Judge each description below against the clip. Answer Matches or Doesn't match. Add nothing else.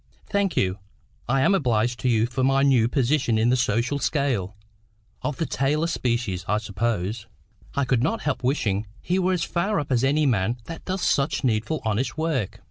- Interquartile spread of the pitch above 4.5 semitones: Matches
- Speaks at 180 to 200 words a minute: Matches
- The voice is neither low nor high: Doesn't match